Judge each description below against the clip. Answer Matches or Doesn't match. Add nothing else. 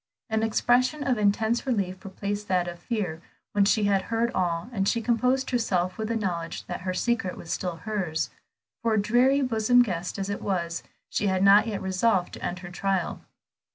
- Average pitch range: Matches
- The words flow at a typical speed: Matches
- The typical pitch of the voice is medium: Doesn't match